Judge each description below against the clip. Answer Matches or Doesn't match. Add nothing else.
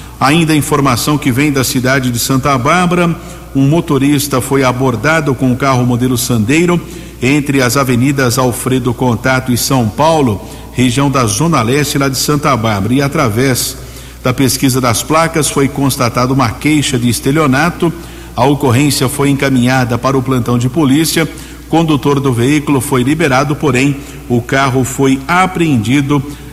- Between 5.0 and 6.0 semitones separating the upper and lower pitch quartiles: Doesn't match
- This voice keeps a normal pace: Matches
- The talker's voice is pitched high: Doesn't match